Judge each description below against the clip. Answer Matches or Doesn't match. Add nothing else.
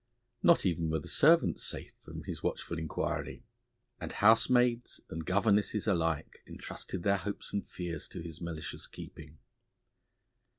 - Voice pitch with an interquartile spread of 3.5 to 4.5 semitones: Matches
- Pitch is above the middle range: Doesn't match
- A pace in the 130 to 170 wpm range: Matches